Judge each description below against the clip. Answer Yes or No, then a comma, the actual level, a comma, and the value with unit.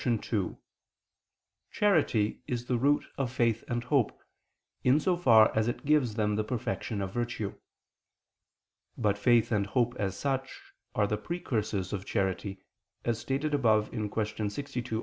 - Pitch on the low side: Yes, low, 115 Hz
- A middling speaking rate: Yes, average, 150 wpm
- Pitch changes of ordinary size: Yes, average, 3.7 semitones